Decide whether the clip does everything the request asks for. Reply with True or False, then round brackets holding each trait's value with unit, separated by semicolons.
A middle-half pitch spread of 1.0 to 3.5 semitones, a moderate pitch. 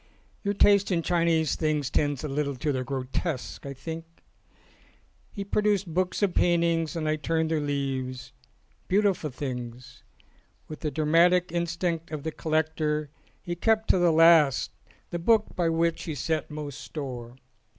True (3.2 semitones; 160 Hz)